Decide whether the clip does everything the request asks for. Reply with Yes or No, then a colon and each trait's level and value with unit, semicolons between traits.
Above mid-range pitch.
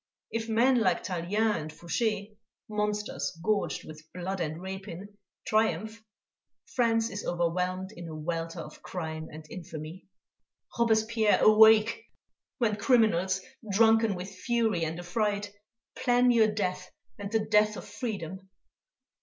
Yes: high, 205 Hz